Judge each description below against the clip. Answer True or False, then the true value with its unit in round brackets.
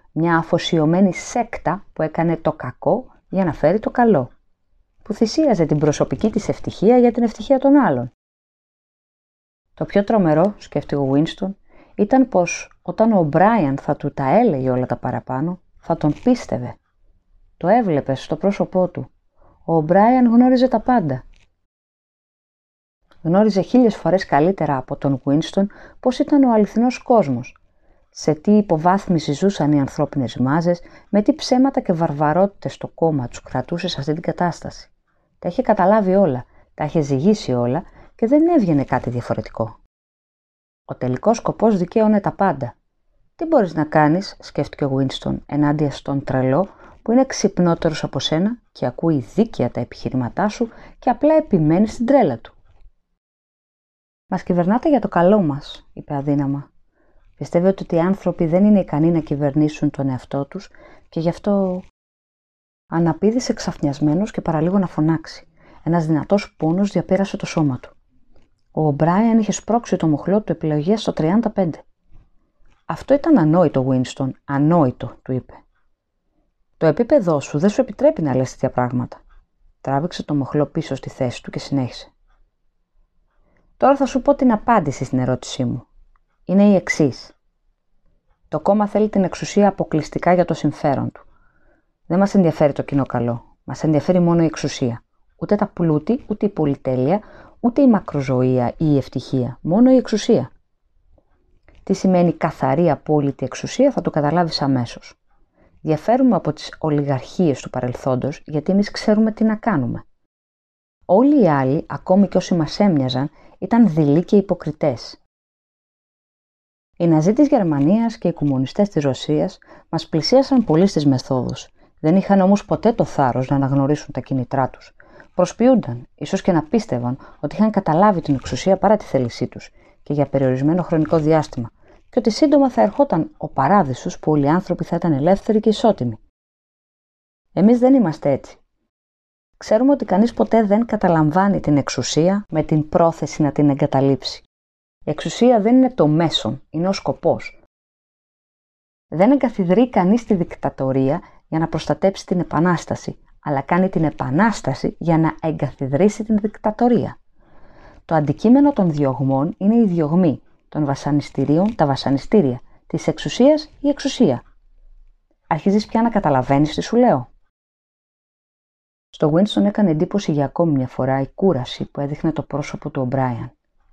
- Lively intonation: True (6.6 semitones)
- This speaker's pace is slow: False (150 wpm)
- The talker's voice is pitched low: False (160 Hz)